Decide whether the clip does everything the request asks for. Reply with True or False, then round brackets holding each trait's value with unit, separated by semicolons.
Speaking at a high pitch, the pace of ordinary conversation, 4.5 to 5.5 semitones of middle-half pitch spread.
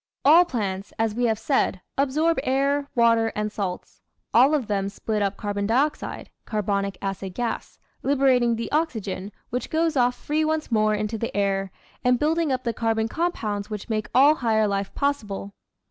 True (230 Hz; 170 wpm; 5.2 semitones)